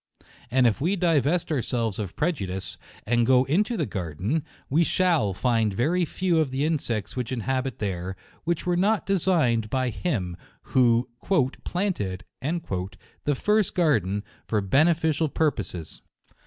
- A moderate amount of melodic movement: No, wide, 7.7 semitones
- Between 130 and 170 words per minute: Yes, average, 140 wpm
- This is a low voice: Yes, low, 130 Hz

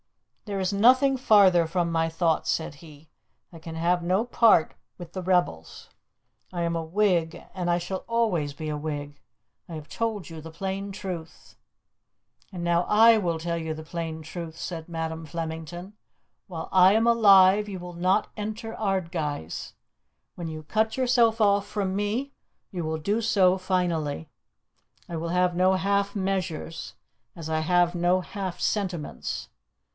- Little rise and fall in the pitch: No, average, 3.6 semitones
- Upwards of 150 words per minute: Yes, average, 160 wpm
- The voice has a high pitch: No, medium, 180 Hz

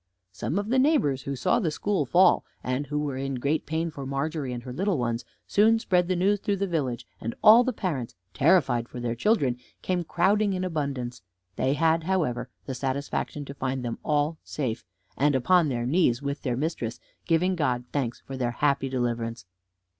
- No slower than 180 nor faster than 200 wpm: Yes, average, 190 wpm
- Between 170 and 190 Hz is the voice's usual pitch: No, medium, 145 Hz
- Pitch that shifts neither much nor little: No, wide, 6.0 semitones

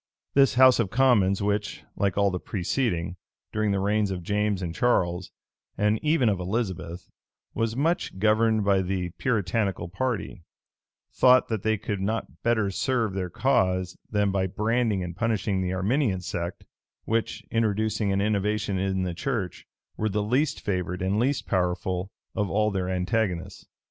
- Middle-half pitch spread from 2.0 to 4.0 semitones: Yes, average, 3.3 semitones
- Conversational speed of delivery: Yes, average, 155 wpm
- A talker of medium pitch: No, low, 100 Hz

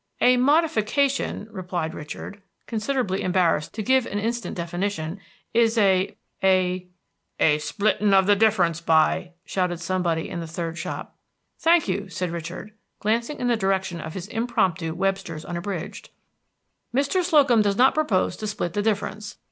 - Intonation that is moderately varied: Yes, average, 4.4 semitones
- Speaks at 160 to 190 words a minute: No, average, 150 wpm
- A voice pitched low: No, high, 195 Hz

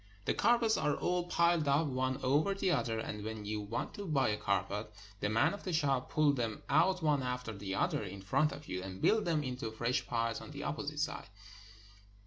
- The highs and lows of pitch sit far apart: Yes, wide, 6.1 semitones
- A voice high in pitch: No, low, 135 Hz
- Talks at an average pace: No, fast, 215 wpm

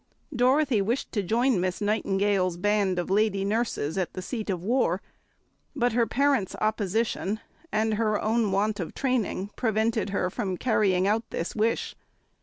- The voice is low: No, high, 215 Hz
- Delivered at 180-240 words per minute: No, average, 155 wpm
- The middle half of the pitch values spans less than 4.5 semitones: Yes, average, 3.0 semitones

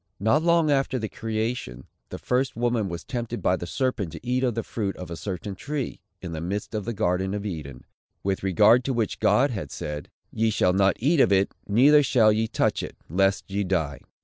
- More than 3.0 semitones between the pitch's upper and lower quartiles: Yes, average, 4.7 semitones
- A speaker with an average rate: No, fast, 215 wpm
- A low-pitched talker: Yes, low, 105 Hz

